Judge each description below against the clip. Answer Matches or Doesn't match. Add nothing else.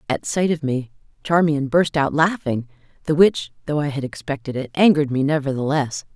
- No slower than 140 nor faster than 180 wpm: Matches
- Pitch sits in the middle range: Matches